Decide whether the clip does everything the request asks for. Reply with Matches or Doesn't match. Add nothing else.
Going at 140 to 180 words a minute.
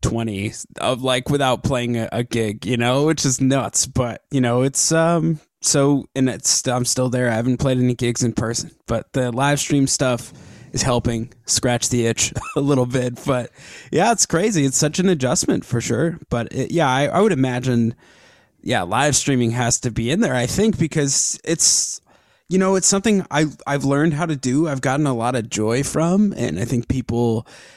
Doesn't match